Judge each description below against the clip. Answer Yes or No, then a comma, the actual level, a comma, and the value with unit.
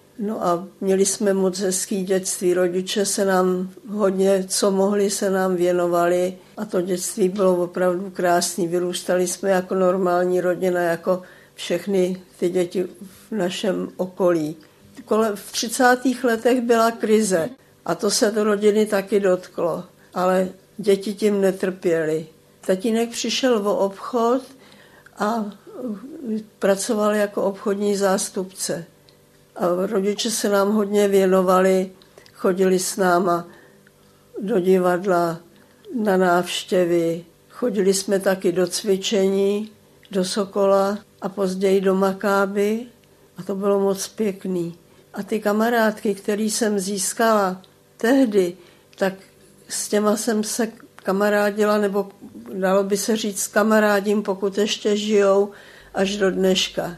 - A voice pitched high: Yes, high, 195 Hz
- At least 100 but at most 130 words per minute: Yes, average, 120 wpm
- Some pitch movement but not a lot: No, narrow, 2.2 semitones